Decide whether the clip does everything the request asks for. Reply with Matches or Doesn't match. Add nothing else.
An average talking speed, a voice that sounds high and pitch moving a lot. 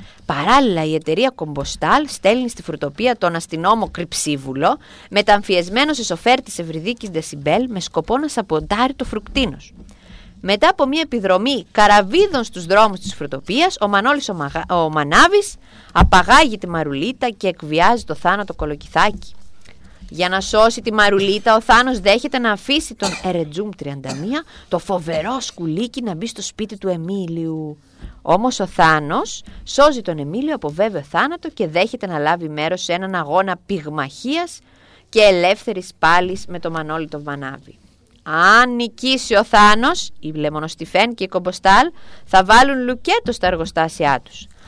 Matches